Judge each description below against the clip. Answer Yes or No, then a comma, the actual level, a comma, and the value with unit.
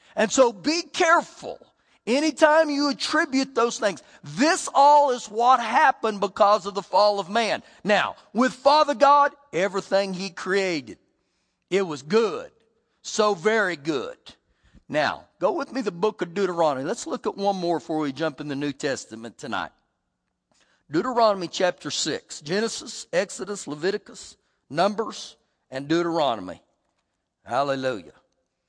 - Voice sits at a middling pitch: No, high, 210 Hz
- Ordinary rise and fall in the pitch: No, wide, 7.2 semitones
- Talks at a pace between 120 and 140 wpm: Yes, slow, 135 wpm